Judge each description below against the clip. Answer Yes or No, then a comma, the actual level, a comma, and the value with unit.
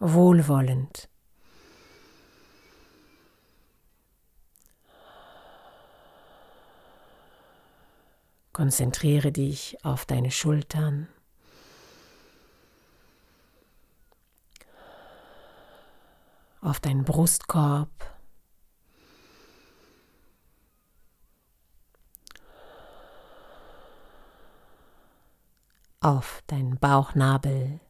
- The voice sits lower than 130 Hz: No, medium, 140 Hz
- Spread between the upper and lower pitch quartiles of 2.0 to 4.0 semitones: Yes, average, 2.8 semitones